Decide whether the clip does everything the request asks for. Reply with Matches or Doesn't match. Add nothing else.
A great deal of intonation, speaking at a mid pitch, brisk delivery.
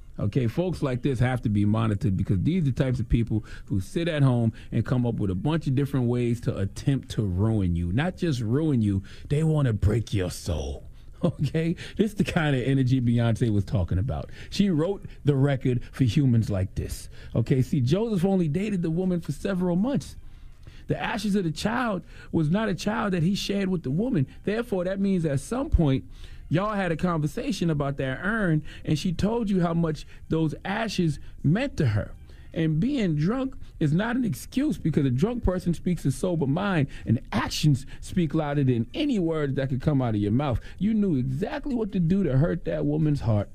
Matches